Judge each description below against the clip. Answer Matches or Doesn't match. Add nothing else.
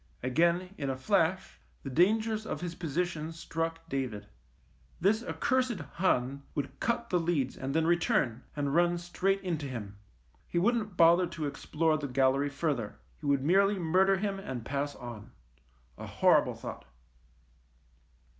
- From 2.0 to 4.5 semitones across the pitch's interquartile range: Doesn't match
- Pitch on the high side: Doesn't match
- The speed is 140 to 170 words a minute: Matches